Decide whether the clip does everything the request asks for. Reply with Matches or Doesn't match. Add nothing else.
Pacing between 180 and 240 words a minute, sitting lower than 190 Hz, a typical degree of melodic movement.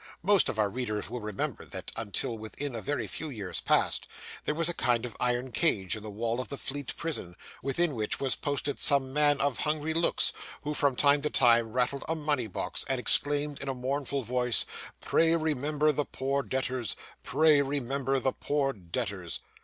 Matches